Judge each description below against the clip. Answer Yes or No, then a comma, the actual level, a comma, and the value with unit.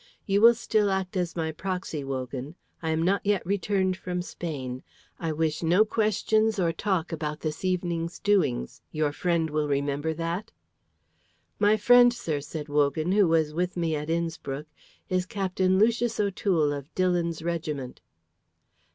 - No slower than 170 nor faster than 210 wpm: No, average, 150 wpm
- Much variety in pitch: No, average, 4.0 semitones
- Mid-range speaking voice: Yes, medium, 170 Hz